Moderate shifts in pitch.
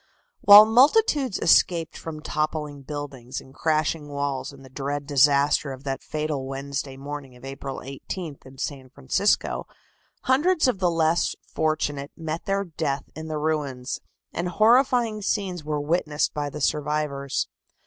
Yes: average, 3.6 semitones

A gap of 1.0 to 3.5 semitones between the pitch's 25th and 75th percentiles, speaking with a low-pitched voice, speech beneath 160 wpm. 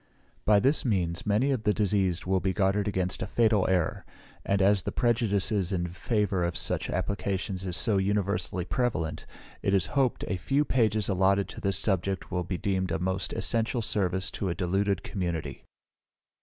No: narrow, 2.4 semitones; very low, 95 Hz; average, 175 wpm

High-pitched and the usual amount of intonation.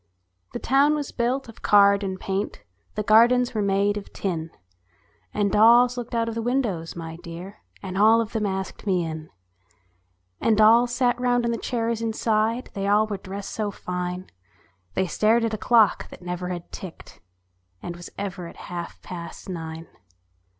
Yes: high, 210 Hz; average, 3.8 semitones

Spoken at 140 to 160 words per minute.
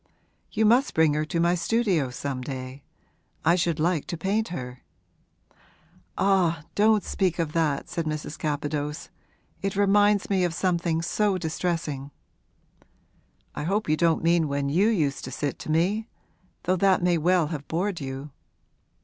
Yes: average, 155 wpm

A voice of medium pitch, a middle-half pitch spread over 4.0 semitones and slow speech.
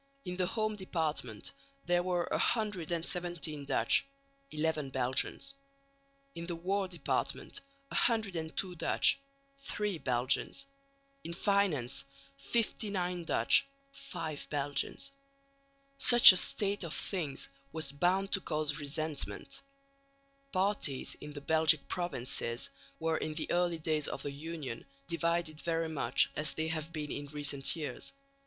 No: medium, 165 Hz; average, 3.7 semitones; slow, 120 wpm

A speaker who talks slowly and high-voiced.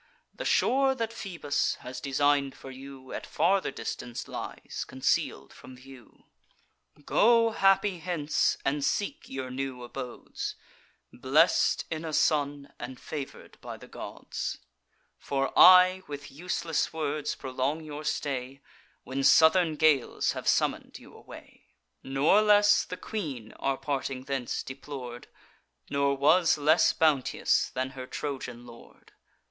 No: slow, 130 wpm; medium, 145 Hz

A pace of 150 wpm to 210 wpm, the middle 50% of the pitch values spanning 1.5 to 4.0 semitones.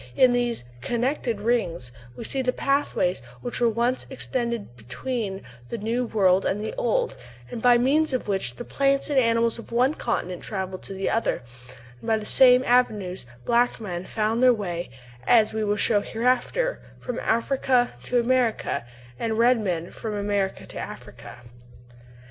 Yes: average, 160 wpm; average, 3.6 semitones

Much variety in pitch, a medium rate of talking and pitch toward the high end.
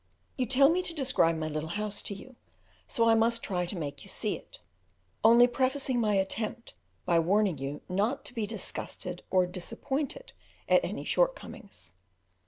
Yes: wide, 6.1 semitones; average, 170 wpm; high, 220 Hz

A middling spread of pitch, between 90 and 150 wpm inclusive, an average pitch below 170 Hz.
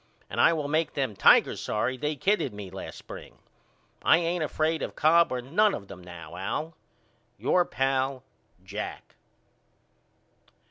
No: wide, 7.6 semitones; average, 145 wpm; low, 135 Hz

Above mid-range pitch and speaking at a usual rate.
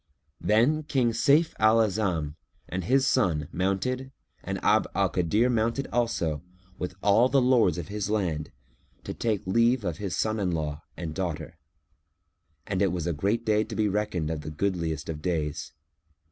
No: low, 100 Hz; average, 165 wpm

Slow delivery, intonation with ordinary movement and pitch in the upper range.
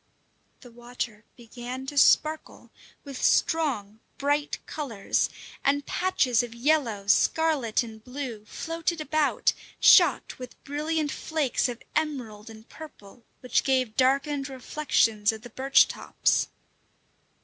Yes: slow, 115 wpm; average, 4.4 semitones; very high, 260 Hz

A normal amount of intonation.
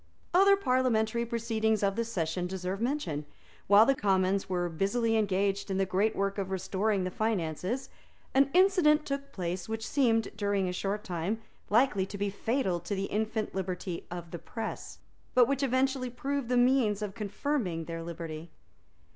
Yes: average, 4.6 semitones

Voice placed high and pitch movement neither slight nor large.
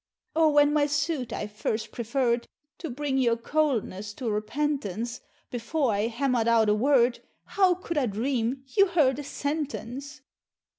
Yes: very high, 260 Hz; average, 4.1 semitones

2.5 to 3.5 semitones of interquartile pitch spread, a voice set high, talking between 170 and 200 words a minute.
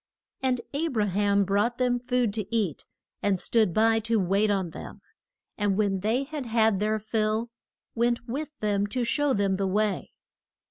Yes: average, 3.0 semitones; high, 215 Hz; average, 175 wpm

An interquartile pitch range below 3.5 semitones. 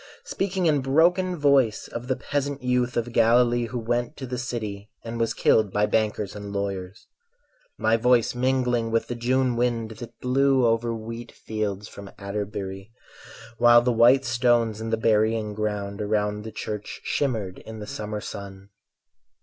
Yes: average, 2.8 semitones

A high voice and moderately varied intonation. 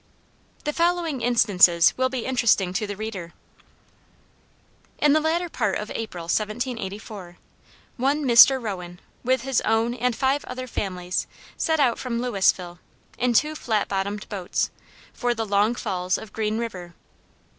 Yes: high, 225 Hz; average, 4.8 semitones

